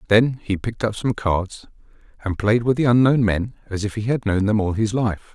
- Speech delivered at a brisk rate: Yes, fast, 235 wpm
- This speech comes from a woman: No, male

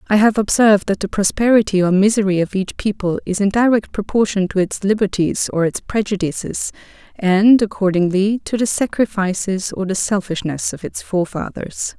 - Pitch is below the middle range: No, high, 200 Hz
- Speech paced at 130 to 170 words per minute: Yes, average, 160 wpm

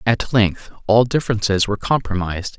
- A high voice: No, low, 110 Hz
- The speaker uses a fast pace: No, average, 140 wpm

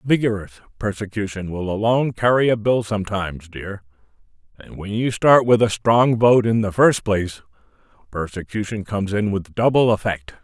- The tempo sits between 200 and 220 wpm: No, average, 155 wpm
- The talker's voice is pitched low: Yes, low, 105 Hz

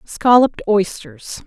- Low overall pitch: No, high, 200 Hz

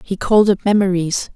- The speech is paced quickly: No, average, 175 wpm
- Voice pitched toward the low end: No, high, 195 Hz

